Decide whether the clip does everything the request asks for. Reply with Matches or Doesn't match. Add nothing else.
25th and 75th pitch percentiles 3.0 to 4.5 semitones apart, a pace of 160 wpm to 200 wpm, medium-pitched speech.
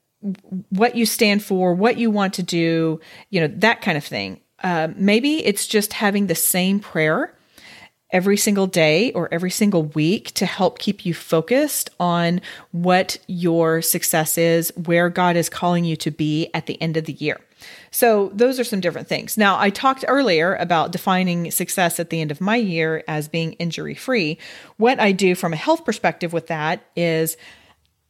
Matches